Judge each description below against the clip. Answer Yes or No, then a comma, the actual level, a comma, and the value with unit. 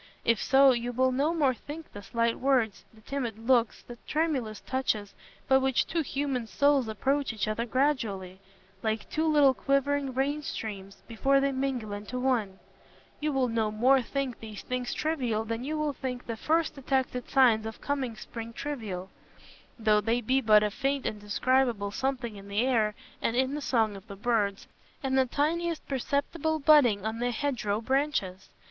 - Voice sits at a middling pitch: No, very high, 250 Hz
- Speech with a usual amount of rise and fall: Yes, average, 4.0 semitones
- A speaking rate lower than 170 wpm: No, average, 175 wpm